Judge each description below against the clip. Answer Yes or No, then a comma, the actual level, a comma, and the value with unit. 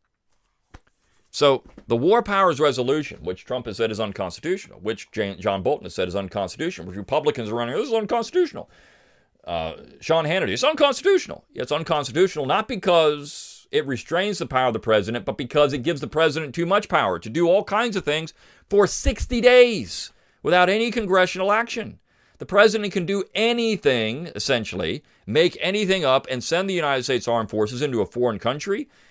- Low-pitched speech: No, medium, 170 Hz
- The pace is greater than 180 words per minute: No, average, 175 wpm